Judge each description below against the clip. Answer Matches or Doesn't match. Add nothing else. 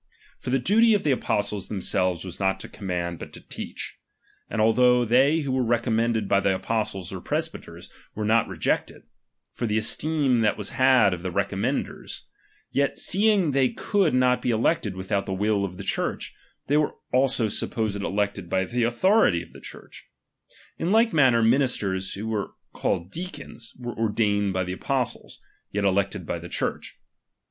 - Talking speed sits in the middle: Matches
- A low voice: Matches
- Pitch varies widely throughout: Doesn't match